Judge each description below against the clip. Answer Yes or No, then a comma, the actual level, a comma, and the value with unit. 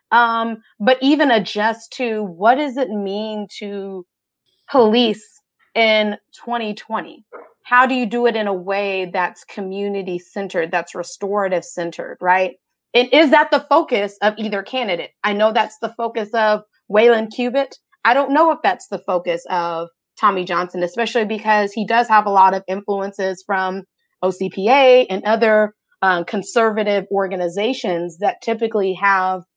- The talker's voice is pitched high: Yes, high, 210 Hz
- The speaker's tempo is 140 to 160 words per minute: Yes, average, 150 wpm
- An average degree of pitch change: Yes, average, 3.3 semitones